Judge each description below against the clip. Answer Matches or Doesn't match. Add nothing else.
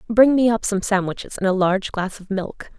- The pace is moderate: Doesn't match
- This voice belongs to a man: Doesn't match